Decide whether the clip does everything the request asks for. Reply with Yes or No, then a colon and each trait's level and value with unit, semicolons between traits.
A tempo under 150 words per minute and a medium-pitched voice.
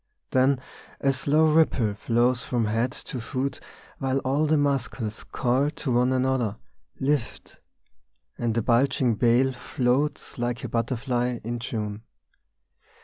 No: slow, 135 wpm; low, 125 Hz